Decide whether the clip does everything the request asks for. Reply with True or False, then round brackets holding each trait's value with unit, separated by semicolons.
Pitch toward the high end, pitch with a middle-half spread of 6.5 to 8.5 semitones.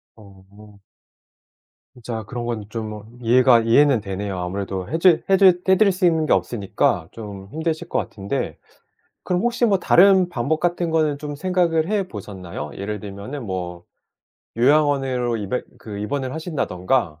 False (125 Hz; 7.9 semitones)